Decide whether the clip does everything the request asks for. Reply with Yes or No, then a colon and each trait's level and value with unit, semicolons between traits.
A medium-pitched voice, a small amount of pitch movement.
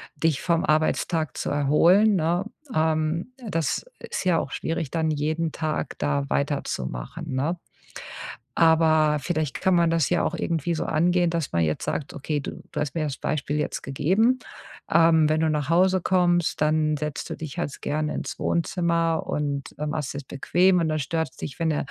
Yes: medium, 155 Hz; narrow, 2.3 semitones